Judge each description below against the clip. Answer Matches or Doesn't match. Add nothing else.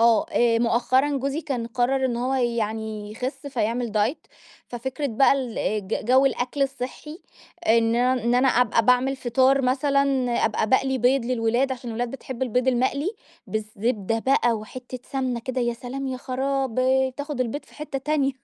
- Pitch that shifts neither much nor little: Doesn't match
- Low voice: Doesn't match